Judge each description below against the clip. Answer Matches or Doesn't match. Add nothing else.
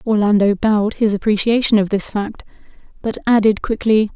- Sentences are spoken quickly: Doesn't match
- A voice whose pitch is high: Matches